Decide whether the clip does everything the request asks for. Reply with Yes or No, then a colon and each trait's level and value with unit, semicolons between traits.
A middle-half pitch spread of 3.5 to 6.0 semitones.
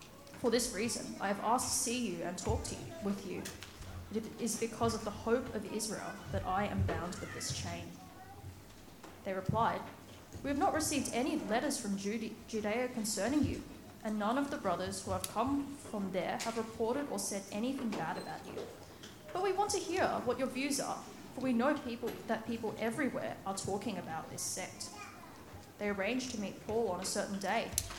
Yes: average, 4.4 semitones